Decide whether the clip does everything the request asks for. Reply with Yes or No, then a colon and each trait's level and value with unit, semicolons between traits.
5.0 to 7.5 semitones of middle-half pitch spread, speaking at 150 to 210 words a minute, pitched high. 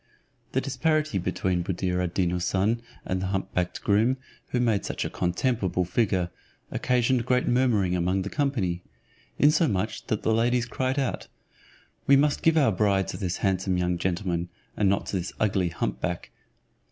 No: average, 5.3 semitones; average, 165 wpm; low, 100 Hz